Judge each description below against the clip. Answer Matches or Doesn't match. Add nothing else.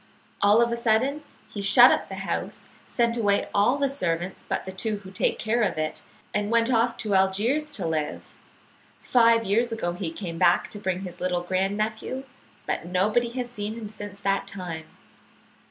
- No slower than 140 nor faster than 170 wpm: Doesn't match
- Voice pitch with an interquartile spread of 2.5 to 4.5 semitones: Matches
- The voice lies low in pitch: Doesn't match